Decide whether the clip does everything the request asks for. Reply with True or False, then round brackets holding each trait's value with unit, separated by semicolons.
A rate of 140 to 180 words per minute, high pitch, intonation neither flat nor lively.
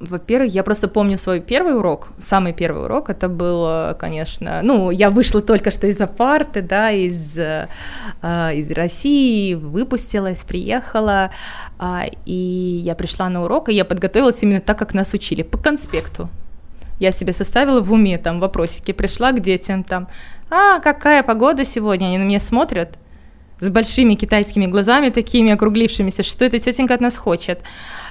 True (160 wpm; 200 Hz; 4.6 semitones)